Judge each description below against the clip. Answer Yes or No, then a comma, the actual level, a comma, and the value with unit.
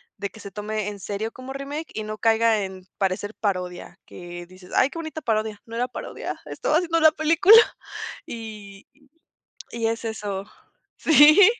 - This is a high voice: Yes, high, 220 Hz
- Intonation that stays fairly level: No, wide, 5.5 semitones